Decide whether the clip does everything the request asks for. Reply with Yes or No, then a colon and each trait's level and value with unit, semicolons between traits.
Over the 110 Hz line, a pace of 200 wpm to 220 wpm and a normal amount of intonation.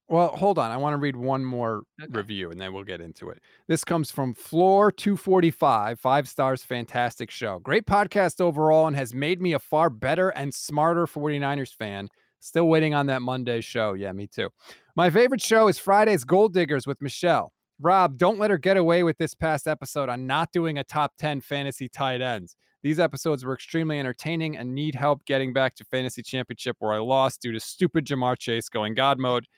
Yes: medium, 140 Hz; fast, 205 wpm; average, 4.8 semitones